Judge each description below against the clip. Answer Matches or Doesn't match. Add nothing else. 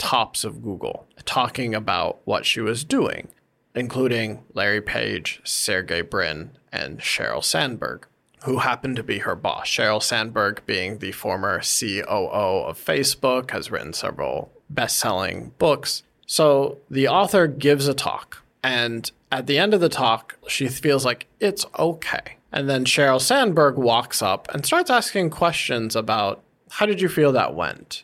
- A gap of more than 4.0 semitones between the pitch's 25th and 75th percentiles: Matches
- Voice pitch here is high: Doesn't match